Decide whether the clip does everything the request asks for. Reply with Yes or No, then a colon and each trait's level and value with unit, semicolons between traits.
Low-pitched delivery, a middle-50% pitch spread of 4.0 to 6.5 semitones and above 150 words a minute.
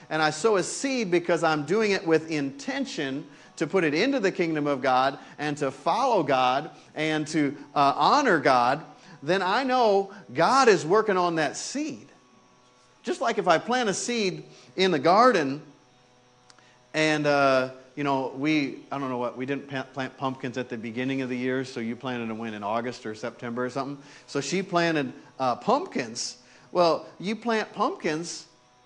No: medium, 145 Hz; average, 5.2 semitones; average, 180 wpm